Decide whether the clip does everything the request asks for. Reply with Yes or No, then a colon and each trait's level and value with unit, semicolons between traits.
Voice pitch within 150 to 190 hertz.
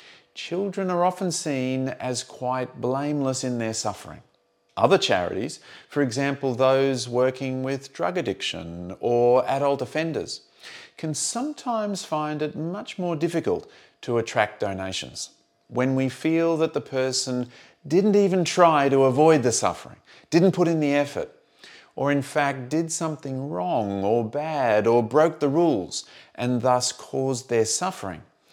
No: low, 135 Hz